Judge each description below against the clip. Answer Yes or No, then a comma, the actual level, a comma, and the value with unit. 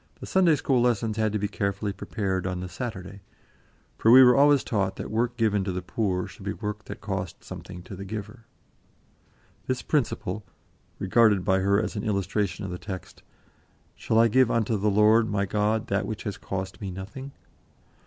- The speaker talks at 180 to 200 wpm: Yes, average, 190 wpm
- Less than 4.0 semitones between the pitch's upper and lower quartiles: Yes, average, 2.7 semitones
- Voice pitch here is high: No, low, 105 Hz